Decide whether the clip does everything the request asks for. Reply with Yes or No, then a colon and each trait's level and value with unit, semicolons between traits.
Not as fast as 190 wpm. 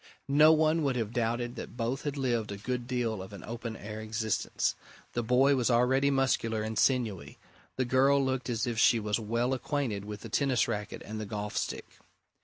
No: average, 200 wpm